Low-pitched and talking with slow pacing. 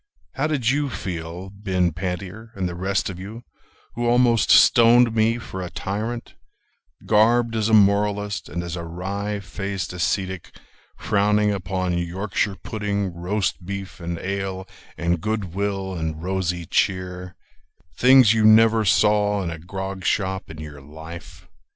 No: very low, 95 Hz; average, 145 wpm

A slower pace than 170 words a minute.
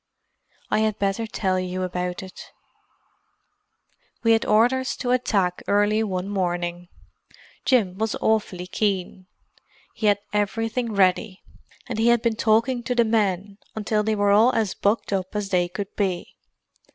Yes: average, 150 wpm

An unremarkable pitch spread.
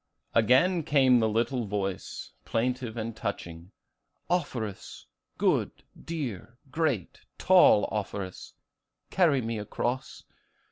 Yes: average, 4.6 semitones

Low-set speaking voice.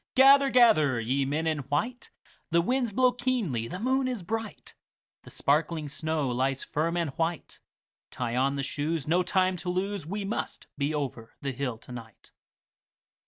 No: medium, 160 Hz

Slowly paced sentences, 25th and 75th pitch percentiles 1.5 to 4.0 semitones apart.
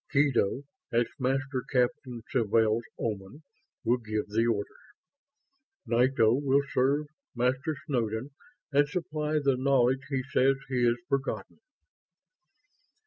Yes: slow, 110 wpm; average, 2.9 semitones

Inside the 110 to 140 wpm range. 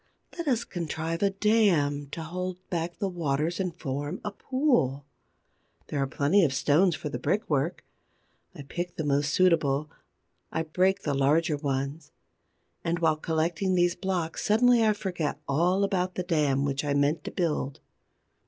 No: average, 160 wpm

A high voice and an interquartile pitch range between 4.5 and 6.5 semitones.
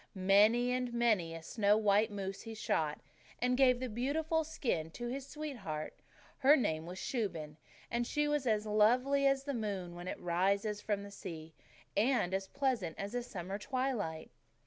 Yes: high, 215 Hz; average, 5.1 semitones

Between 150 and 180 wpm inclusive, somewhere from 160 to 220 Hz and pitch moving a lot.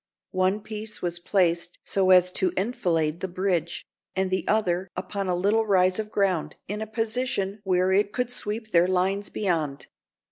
No: average, 170 wpm; high, 190 Hz; narrow, 2.6 semitones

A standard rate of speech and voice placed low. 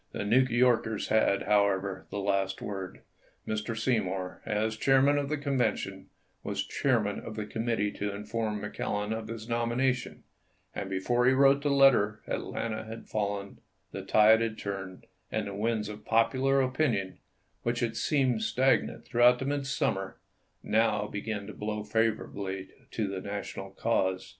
Yes: average, 155 wpm; low, 110 Hz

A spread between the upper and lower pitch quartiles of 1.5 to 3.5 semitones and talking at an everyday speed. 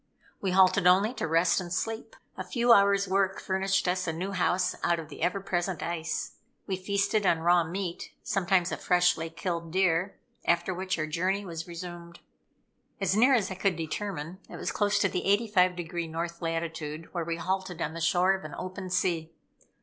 Yes: narrow, 2.4 semitones; average, 190 wpm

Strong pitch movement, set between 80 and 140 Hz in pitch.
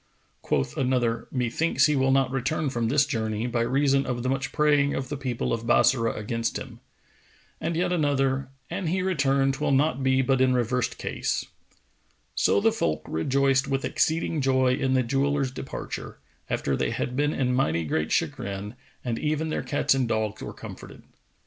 No: average, 2.9 semitones; low, 135 Hz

